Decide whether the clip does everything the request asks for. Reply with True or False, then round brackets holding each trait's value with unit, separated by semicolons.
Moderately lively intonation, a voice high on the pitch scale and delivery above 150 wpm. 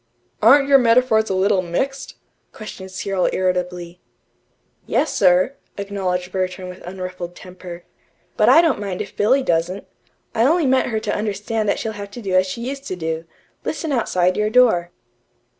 True (4.2 semitones; 195 Hz; 165 wpm)